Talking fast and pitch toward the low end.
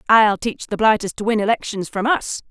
No: fast, 215 wpm; high, 215 Hz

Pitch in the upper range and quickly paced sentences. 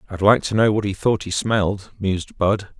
No: low, 100 Hz; fast, 235 wpm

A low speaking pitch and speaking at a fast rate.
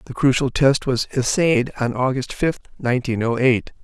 No: low, 130 Hz; average, 170 wpm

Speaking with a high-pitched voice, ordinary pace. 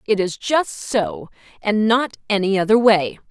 Yes: high, 215 Hz; average, 165 wpm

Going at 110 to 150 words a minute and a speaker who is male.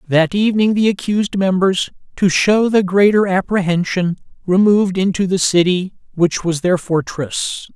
Yes: average, 140 wpm; male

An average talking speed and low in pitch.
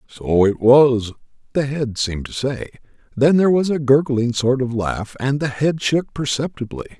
Yes: average, 180 wpm; low, 130 Hz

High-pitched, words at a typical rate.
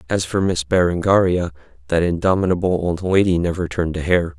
No: very low, 90 Hz; average, 165 wpm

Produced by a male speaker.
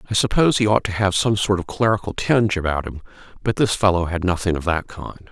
Yes: male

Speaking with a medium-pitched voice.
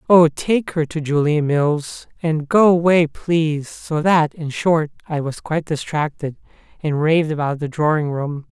Yes: medium, 155 Hz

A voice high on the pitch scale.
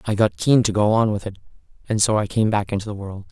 No: low, 105 Hz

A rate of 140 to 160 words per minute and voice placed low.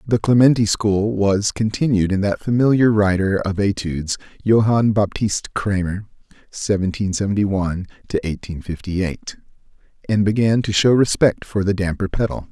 Yes: average, 145 wpm; low, 100 Hz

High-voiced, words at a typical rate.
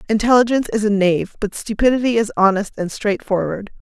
Yes: high, 215 Hz; average, 150 wpm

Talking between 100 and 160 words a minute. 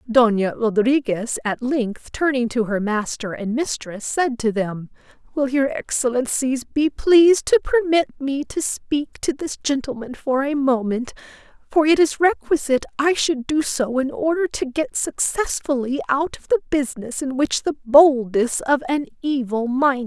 No: average, 175 wpm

